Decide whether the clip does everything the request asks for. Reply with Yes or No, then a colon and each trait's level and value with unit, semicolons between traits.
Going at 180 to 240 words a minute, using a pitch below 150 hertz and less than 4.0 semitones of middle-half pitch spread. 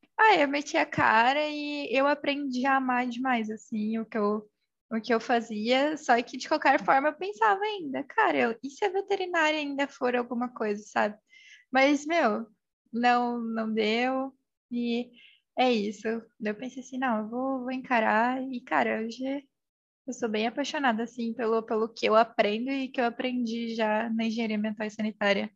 No: fast, 185 wpm; high, 245 Hz; average, 3.6 semitones